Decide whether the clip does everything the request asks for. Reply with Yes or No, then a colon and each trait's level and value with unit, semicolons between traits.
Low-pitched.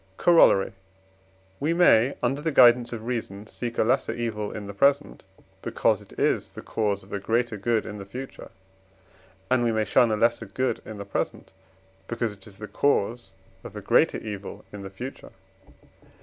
Yes: low, 115 Hz